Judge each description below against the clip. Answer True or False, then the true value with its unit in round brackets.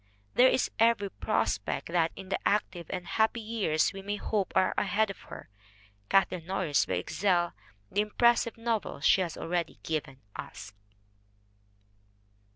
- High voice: True (195 Hz)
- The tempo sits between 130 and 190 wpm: True (145 wpm)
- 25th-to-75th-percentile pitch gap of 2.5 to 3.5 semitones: False (4.1 semitones)